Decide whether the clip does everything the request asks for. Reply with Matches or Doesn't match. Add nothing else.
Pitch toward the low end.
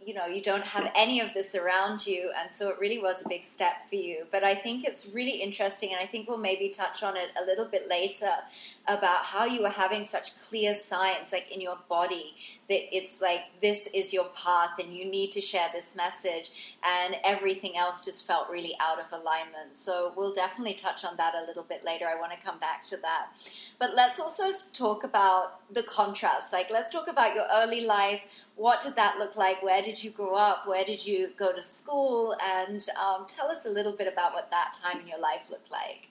Doesn't match